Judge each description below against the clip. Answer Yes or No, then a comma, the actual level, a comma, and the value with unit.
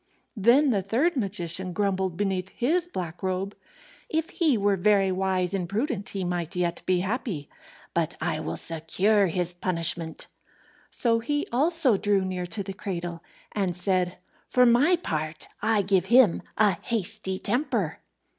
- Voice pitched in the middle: No, high, 195 Hz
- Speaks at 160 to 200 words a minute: No, average, 150 wpm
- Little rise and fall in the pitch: No, average, 4.3 semitones